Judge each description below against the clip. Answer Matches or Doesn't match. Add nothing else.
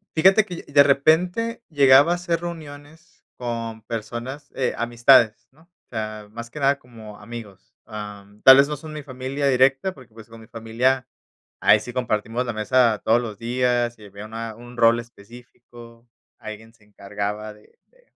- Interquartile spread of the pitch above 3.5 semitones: Matches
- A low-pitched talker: Matches